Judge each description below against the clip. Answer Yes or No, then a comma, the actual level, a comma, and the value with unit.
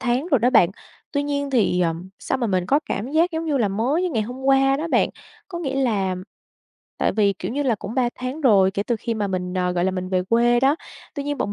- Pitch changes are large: Yes, wide, 6.2 semitones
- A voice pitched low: No, high, 240 Hz